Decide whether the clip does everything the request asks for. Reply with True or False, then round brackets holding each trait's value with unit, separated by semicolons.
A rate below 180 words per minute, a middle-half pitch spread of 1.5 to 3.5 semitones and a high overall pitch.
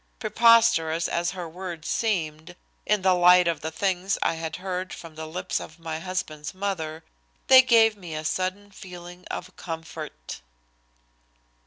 False (150 wpm; 2.9 semitones; 180 Hz)